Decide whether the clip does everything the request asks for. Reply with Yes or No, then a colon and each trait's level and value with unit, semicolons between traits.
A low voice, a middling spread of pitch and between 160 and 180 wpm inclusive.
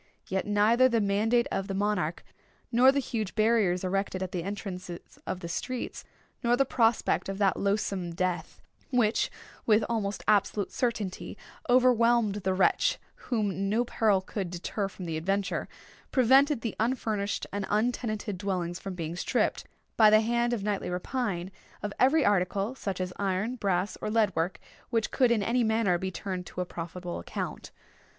No: high, 205 Hz; average, 3.8 semitones; average, 165 wpm